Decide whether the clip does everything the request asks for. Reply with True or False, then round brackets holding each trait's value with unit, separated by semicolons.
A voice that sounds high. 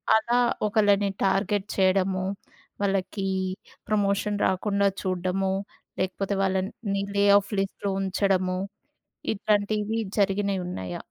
True (195 Hz)